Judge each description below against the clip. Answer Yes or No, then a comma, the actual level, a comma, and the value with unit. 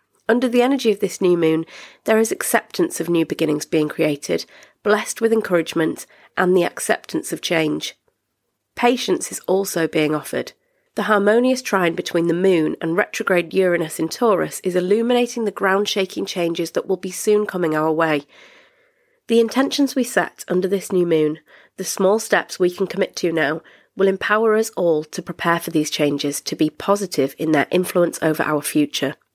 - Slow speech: No, average, 175 wpm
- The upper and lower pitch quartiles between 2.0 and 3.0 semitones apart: No, average, 4.9 semitones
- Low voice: No, medium, 185 Hz